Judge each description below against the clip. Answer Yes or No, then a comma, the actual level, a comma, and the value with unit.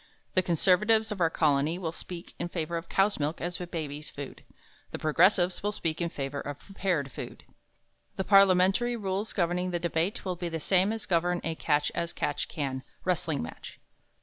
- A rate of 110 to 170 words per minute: No, average, 185 wpm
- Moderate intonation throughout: Yes, average, 3.1 semitones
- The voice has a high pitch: No, medium, 175 Hz